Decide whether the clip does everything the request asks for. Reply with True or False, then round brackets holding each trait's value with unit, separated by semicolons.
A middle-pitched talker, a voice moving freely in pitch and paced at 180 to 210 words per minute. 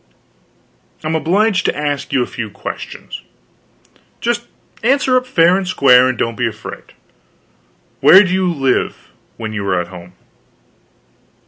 False (150 Hz; 8.3 semitones; 140 wpm)